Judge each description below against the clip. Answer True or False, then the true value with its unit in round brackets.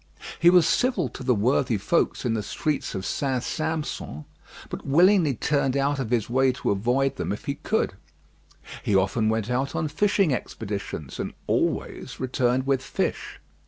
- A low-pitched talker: True (130 Hz)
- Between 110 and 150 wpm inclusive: False (165 wpm)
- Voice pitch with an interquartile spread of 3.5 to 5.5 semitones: True (4.8 semitones)